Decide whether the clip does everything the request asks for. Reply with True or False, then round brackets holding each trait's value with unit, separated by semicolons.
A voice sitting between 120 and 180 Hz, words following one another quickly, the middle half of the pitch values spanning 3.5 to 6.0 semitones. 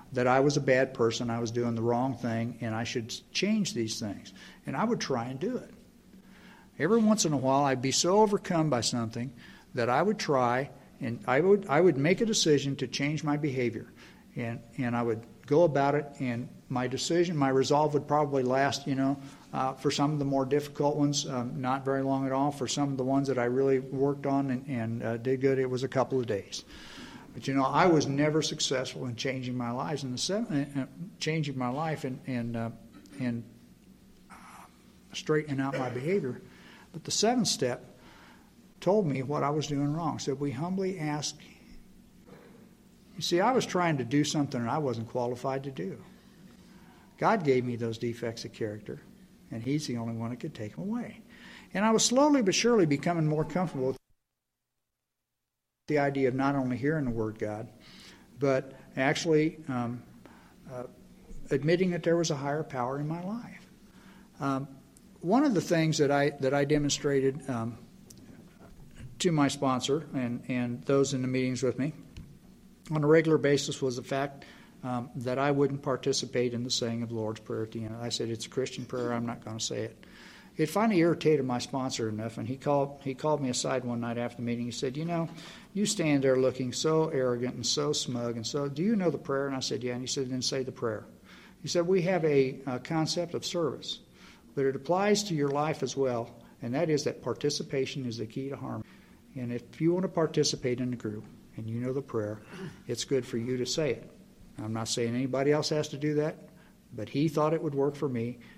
True (135 Hz; 210 wpm; 3.8 semitones)